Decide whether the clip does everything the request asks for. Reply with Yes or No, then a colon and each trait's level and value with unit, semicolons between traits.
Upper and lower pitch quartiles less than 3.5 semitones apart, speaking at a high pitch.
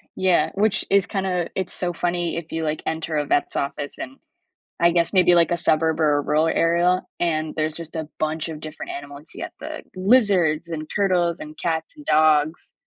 No: narrow, 2.6 semitones; medium, 165 Hz